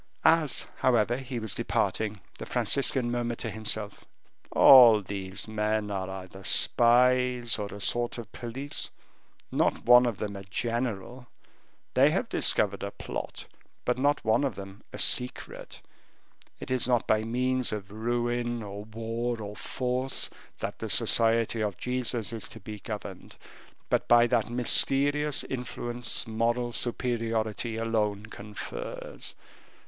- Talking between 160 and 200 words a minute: No, average, 140 wpm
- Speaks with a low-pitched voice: Yes, low, 115 Hz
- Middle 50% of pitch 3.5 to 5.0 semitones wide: No, narrow, 2.5 semitones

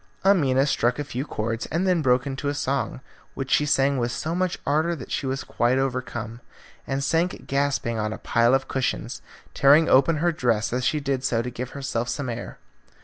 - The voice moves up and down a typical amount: Yes, average, 3.0 semitones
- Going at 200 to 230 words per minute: Yes, fast, 205 wpm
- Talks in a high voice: No, low, 135 Hz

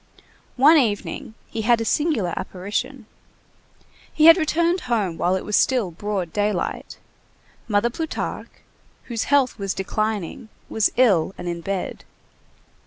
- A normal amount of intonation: Yes, average, 4.8 semitones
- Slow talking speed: Yes, slow, 130 wpm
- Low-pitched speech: No, high, 220 Hz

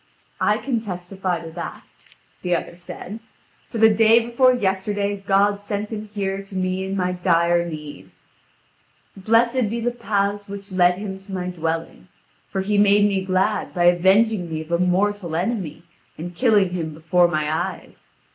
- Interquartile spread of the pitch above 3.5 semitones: No, average, 2.9 semitones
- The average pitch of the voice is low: No, high, 190 Hz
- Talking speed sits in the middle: Yes, average, 165 wpm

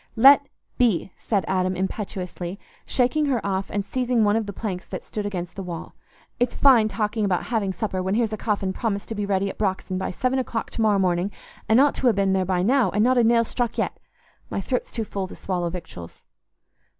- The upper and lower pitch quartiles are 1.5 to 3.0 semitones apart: No, average, 3.7 semitones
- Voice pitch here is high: Yes, high, 205 Hz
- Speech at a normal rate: No, fast, 215 wpm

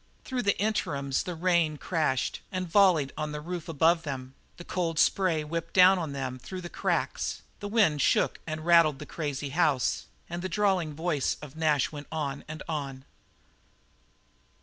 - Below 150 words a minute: No, average, 170 wpm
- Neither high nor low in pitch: Yes, medium, 160 Hz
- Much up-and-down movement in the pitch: No, average, 3.5 semitones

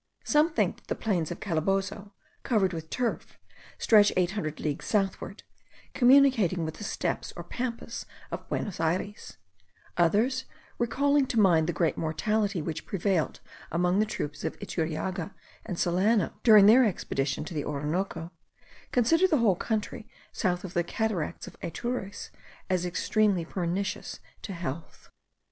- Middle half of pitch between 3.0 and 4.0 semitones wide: No, average, 4.6 semitones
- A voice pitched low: No, high, 195 Hz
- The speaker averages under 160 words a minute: Yes, average, 145 wpm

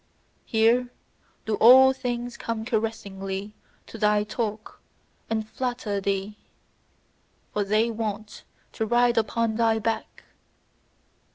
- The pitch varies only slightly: Yes, narrow, 2.0 semitones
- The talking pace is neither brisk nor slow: No, slow, 105 wpm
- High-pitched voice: Yes, high, 220 Hz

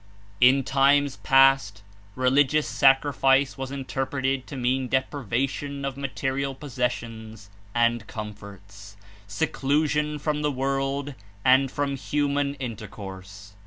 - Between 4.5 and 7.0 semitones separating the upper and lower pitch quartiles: No, average, 3.2 semitones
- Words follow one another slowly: Yes, slow, 110 wpm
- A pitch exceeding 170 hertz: No, low, 135 Hz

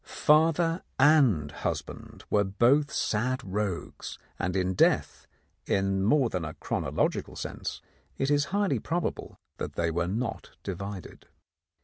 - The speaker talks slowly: Yes, slow, 125 wpm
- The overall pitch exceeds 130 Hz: No, low, 105 Hz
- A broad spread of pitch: Yes, wide, 7.7 semitones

